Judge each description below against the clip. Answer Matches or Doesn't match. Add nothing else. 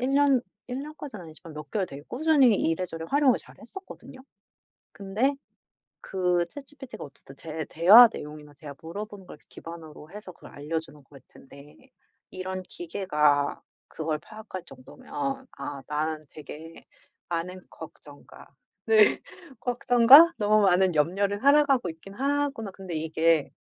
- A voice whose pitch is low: Doesn't match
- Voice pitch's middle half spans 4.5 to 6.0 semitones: Doesn't match